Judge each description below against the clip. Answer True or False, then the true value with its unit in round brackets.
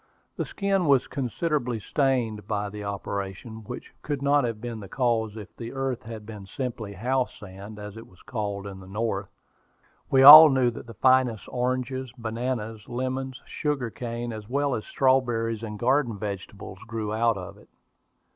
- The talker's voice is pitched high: False (115 Hz)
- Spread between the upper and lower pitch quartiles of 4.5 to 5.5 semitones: False (3.7 semitones)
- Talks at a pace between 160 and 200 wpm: True (170 wpm)